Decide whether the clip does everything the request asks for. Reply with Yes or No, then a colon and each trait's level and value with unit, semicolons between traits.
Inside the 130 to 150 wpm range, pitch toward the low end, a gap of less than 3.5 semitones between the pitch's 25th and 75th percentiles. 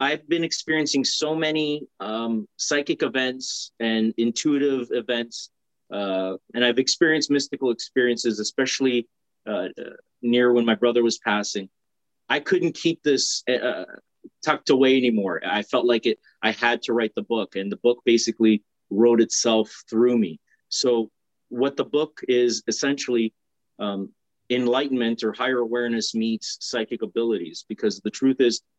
Yes: average, 145 wpm; low, 120 Hz; average, 2.9 semitones